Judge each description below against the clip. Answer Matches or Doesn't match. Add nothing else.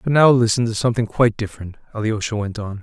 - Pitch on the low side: Matches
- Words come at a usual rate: Doesn't match